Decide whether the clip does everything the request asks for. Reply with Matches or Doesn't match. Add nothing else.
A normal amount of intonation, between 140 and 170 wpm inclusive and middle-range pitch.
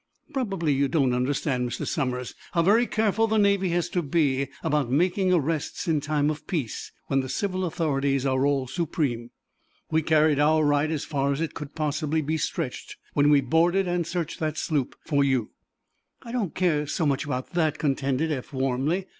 Doesn't match